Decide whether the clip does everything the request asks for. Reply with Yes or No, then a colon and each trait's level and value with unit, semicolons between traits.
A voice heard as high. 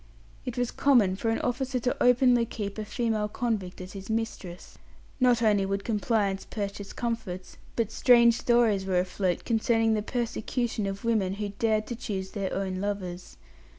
Yes: high, 215 Hz